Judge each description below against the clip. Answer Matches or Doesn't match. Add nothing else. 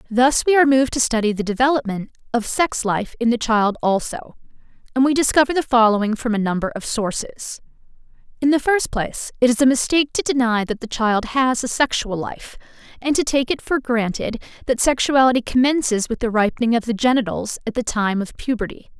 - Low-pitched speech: Doesn't match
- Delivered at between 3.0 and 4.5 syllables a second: Doesn't match